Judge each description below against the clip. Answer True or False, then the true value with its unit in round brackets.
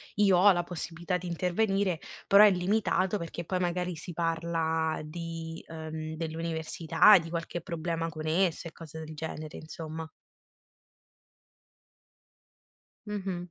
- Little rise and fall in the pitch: True (2.1 semitones)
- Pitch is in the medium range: True (165 Hz)